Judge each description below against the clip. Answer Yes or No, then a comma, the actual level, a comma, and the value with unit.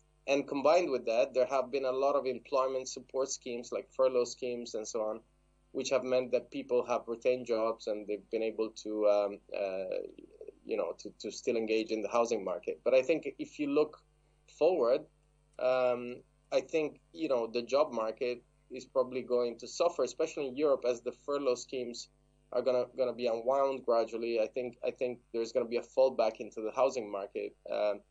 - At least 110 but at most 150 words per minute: No, average, 195 wpm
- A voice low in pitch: Yes, low, 125 Hz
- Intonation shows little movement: No, average, 4.1 semitones